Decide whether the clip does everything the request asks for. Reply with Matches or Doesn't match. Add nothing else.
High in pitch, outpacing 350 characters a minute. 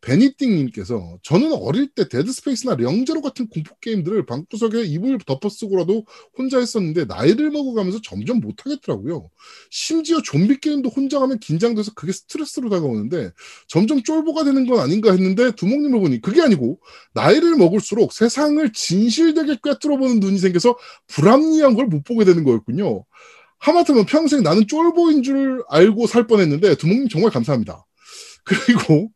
Matches